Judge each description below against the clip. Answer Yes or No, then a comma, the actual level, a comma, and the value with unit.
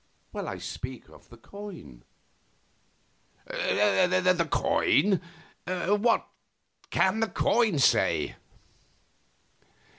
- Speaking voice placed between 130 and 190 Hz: Yes, medium, 185 Hz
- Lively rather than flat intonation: Yes, wide, 7.8 semitones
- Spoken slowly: Yes, slow, 70 wpm